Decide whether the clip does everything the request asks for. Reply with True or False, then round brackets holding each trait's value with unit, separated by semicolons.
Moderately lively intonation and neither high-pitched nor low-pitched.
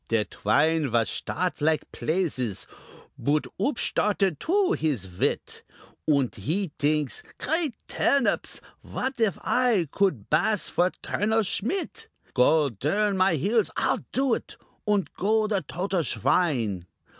False (7.2 semitones; 180 Hz)